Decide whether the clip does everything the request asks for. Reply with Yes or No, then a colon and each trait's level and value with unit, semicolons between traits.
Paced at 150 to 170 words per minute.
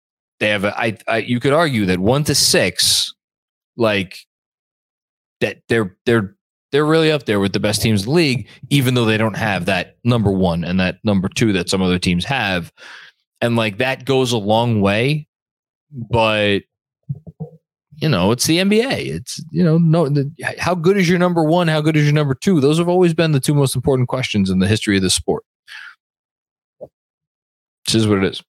No: average, 200 wpm